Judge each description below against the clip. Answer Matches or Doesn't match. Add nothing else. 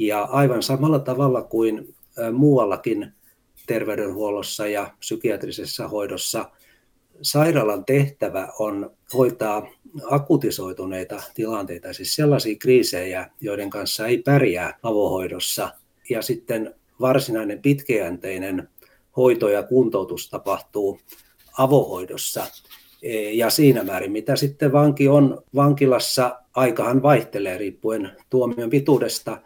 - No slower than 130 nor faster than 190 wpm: Doesn't match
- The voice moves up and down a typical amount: Matches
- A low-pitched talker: Matches